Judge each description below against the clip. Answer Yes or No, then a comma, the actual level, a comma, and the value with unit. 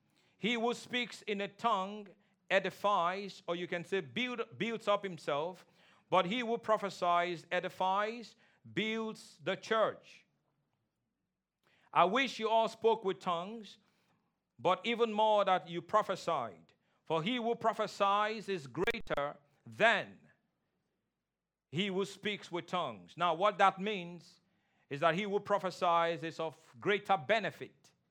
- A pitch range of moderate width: Yes, average, 3.6 semitones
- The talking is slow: Yes, slow, 130 wpm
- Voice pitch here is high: Yes, high, 195 Hz